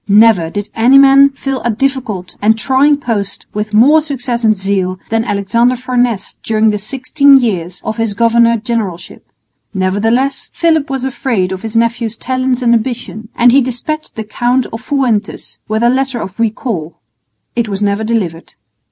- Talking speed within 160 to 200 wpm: Yes, average, 165 wpm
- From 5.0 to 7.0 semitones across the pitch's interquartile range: No, average, 3.7 semitones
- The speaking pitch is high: Yes, high, 230 Hz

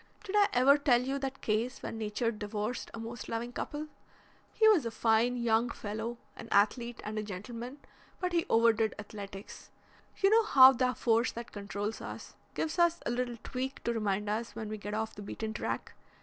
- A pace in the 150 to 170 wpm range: No, average, 190 wpm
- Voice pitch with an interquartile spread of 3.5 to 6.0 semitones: No, average, 3.1 semitones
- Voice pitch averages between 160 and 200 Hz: No, high, 230 Hz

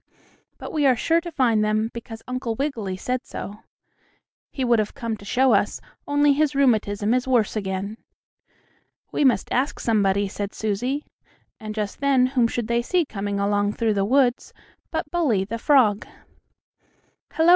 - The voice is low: No, high, 230 Hz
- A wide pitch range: No, average, 4.7 semitones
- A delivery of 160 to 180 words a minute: Yes, average, 165 wpm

